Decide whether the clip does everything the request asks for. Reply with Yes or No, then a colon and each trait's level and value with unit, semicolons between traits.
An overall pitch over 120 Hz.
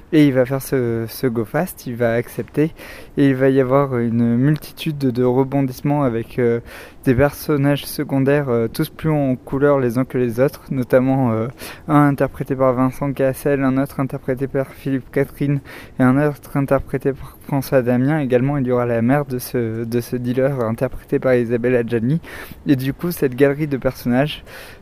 Yes: low, 135 Hz